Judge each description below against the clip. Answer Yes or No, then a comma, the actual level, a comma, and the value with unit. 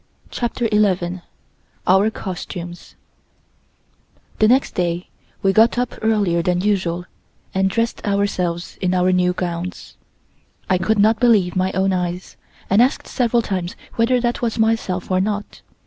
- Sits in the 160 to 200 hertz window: Yes, high, 190 Hz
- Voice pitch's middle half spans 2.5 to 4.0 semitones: Yes, average, 3.5 semitones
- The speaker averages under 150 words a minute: Yes, average, 140 wpm